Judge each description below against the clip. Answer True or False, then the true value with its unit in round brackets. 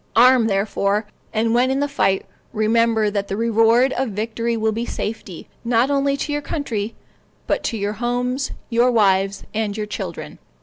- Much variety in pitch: False (2.9 semitones)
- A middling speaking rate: True (170 wpm)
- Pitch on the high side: True (225 Hz)